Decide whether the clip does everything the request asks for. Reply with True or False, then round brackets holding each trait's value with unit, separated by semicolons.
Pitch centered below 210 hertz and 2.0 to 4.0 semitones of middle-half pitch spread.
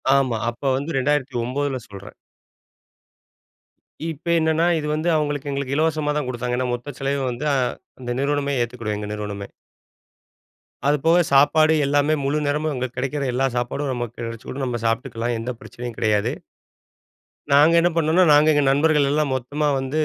True (140 Hz; 3.5 semitones)